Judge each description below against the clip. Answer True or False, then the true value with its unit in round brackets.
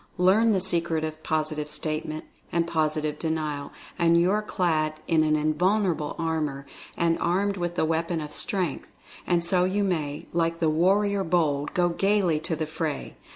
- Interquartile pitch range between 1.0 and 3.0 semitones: True (2.6 semitones)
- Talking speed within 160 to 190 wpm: True (175 wpm)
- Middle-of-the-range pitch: True (165 Hz)